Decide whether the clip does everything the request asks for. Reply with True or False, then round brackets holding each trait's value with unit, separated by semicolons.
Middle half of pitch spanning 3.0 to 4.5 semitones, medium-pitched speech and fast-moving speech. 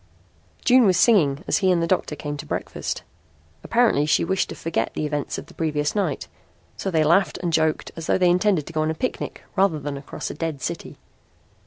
True (3.9 semitones; 165 Hz; 215 wpm)